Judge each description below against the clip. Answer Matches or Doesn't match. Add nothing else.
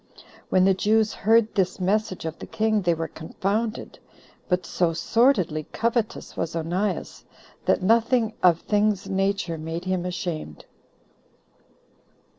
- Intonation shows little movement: Doesn't match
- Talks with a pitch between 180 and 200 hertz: Matches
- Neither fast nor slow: Doesn't match